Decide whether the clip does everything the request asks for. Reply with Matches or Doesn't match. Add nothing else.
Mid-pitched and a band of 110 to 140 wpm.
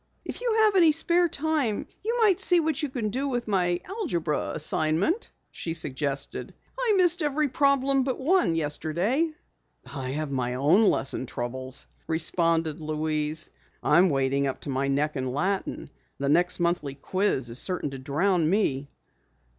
Doesn't match